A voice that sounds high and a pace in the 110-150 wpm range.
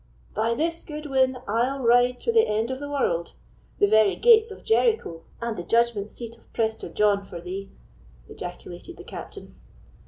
No: high, 235 Hz; average, 165 wpm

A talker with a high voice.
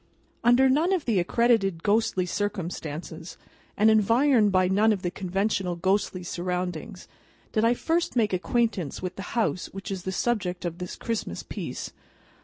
Yes: high, 195 Hz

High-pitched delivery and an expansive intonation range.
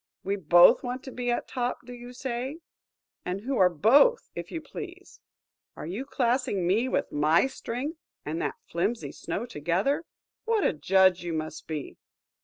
Yes: high, 235 Hz; wide, 7.0 semitones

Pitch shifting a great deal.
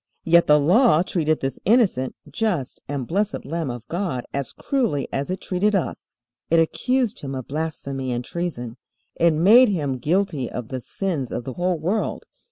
Yes: wide, 6.1 semitones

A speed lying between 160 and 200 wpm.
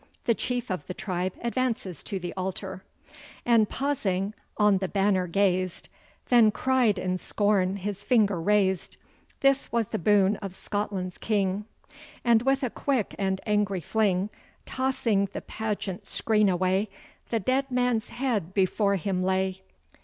No: average, 145 wpm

